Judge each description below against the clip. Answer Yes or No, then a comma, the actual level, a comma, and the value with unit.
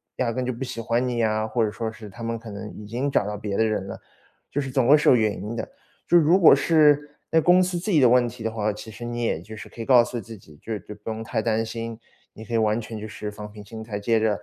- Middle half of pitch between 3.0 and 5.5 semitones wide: No, narrow, 2.6 semitones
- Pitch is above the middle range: No, low, 115 Hz